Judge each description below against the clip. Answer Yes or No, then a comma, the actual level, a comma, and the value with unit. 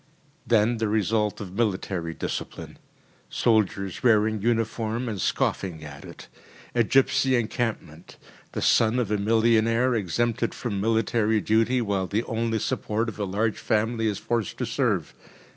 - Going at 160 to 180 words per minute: No, average, 145 wpm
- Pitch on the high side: No, low, 110 Hz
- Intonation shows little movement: Yes, narrow, 2.2 semitones